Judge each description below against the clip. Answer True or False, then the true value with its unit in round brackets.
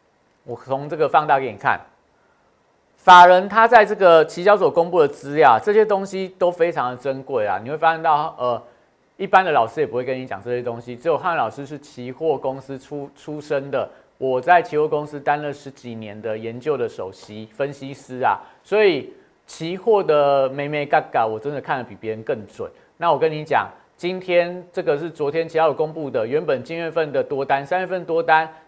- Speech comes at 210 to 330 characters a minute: True (295 characters per minute)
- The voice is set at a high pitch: False (150 Hz)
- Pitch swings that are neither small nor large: True (4.7 semitones)